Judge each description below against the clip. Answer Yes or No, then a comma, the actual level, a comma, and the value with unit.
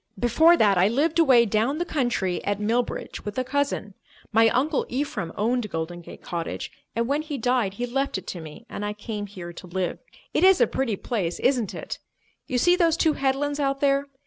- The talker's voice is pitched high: Yes, high, 240 Hz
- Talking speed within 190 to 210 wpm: Yes, fast, 205 wpm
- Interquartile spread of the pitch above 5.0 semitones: Yes, wide, 5.6 semitones